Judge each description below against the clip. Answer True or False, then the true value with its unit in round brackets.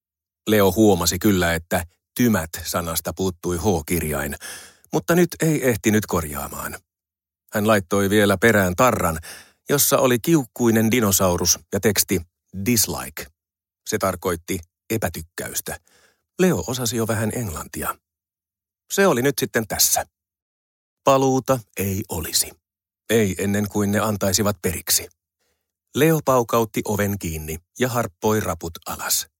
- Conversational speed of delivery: True (110 wpm)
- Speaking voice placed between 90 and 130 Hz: True (100 Hz)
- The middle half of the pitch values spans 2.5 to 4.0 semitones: False (4.8 semitones)